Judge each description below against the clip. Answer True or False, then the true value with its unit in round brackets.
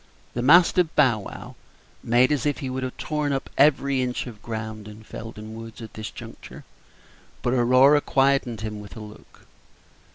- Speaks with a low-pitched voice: True (125 Hz)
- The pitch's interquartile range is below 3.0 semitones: False (3.9 semitones)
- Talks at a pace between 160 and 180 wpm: True (170 wpm)